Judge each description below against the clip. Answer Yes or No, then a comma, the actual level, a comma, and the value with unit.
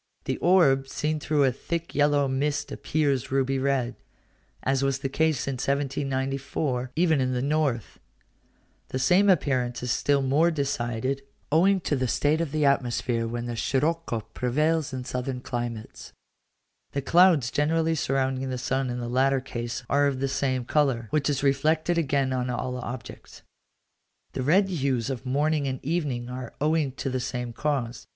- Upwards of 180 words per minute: No, average, 165 wpm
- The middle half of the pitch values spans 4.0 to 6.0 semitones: No, average, 3.0 semitones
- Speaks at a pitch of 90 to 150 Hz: Yes, low, 135 Hz